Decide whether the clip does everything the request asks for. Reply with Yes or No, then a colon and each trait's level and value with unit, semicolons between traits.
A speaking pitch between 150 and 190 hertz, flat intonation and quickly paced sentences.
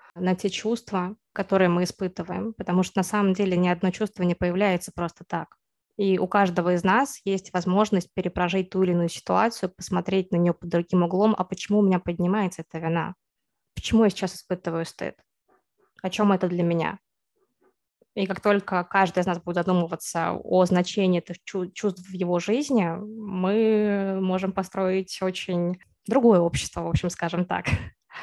Yes: medium, 185 Hz; narrow, 2.1 semitones; fast, 165 wpm